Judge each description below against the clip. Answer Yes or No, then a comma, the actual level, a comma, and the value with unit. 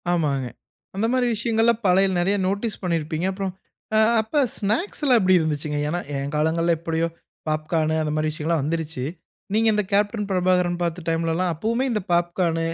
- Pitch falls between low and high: Yes, medium, 175 Hz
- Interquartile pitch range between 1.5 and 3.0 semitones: No, average, 4.3 semitones